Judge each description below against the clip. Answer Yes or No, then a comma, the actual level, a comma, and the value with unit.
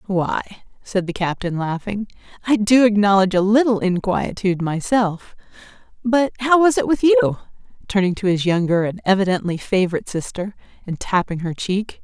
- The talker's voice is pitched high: Yes, high, 200 Hz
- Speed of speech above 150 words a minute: No, average, 145 wpm